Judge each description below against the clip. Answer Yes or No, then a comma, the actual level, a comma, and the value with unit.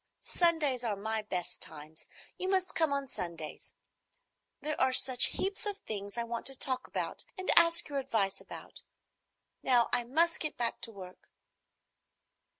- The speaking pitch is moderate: No, very high, 255 Hz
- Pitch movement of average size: No, wide, 7.2 semitones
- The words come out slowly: No, average, 155 wpm